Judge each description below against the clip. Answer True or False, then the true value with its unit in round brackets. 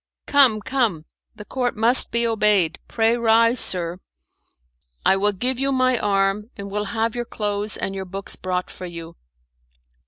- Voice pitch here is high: True (210 Hz)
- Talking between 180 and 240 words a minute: False (160 wpm)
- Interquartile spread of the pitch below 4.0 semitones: True (3.4 semitones)